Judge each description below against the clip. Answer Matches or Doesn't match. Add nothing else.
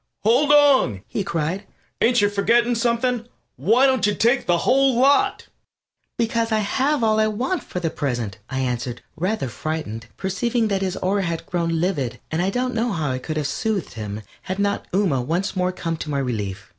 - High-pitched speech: Matches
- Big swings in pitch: Matches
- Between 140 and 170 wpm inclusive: Doesn't match